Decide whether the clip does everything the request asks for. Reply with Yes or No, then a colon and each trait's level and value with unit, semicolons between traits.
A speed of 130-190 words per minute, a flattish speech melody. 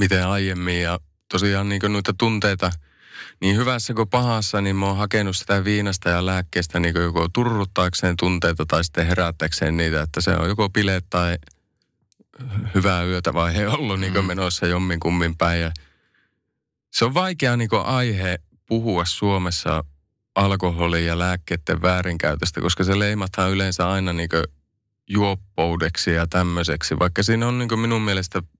No: fast, 155 wpm; average, 3.0 semitones